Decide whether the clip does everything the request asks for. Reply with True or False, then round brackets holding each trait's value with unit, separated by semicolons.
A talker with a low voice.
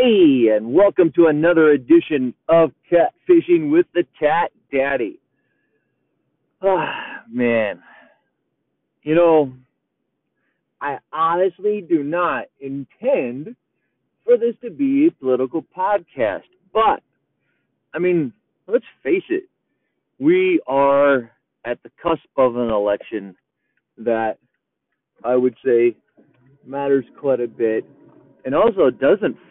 False (160 Hz)